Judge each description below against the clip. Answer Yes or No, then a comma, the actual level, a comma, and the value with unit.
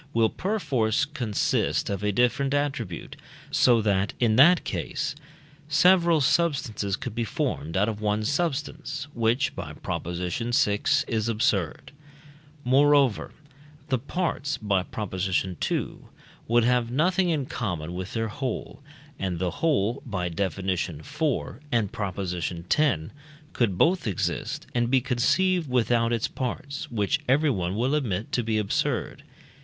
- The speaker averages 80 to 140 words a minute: Yes, slow, 135 wpm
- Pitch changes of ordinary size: No, wide, 6.0 semitones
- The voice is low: Yes, low, 115 Hz